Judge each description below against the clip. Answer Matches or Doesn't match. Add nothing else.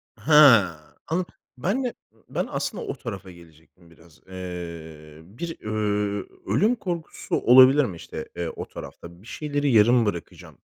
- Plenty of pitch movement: Matches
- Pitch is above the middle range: Doesn't match